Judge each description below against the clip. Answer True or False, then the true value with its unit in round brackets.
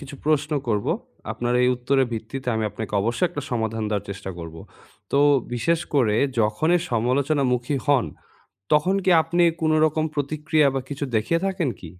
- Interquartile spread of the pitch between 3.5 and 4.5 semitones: False (5.3 semitones)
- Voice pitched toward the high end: False (135 Hz)